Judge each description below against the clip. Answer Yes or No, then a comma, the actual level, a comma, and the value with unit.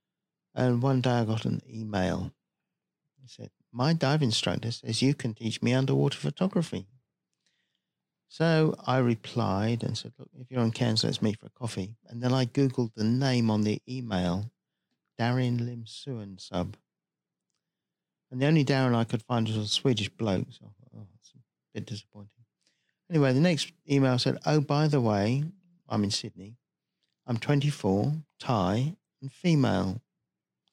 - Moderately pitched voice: No, low, 125 Hz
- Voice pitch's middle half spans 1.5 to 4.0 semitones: No, average, 4.4 semitones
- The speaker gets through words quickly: No, average, 155 wpm